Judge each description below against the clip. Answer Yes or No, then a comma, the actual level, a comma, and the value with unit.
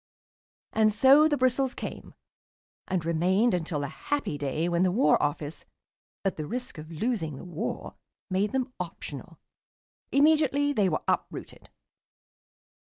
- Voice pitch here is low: No, high, 190 Hz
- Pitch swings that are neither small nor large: No, wide, 8.1 semitones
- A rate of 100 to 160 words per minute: Yes, slow, 135 wpm